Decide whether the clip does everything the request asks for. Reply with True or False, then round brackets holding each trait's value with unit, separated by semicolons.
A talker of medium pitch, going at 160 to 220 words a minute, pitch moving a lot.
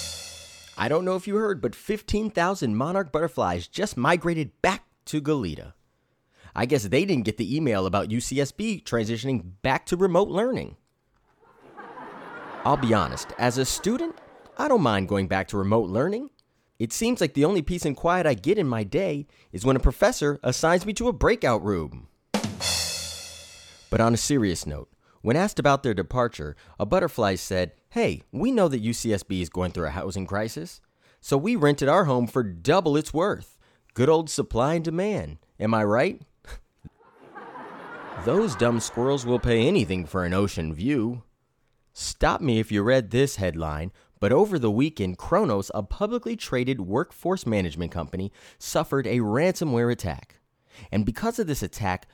False (120 Hz; 165 wpm; 8.9 semitones)